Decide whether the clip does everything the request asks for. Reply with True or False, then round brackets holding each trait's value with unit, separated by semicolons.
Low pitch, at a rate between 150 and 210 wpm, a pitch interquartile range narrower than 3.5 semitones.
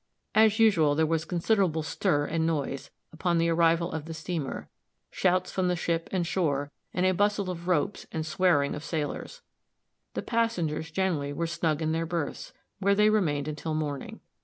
False (165 Hz; 175 wpm; 3.1 semitones)